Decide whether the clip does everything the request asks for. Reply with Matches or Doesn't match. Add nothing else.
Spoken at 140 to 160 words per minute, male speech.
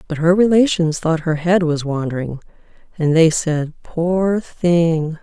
Doesn't match